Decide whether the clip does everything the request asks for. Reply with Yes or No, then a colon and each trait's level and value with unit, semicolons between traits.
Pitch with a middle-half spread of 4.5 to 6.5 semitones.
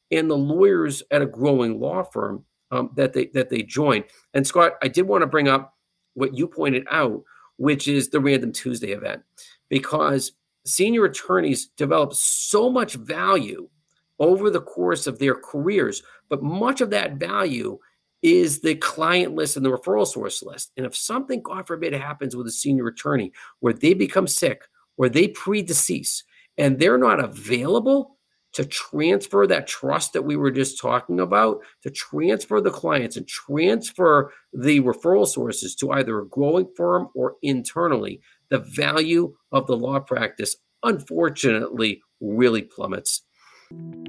Yes: average, 5.3 semitones